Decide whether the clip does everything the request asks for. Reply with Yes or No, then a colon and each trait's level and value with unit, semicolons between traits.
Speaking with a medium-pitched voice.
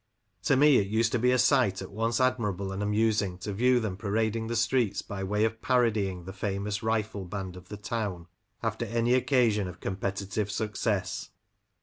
No: low, 105 Hz